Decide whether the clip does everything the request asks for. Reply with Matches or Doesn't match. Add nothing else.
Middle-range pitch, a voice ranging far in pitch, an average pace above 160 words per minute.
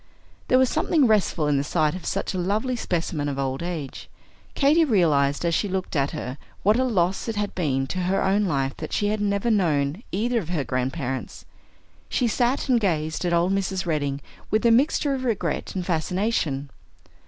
Matches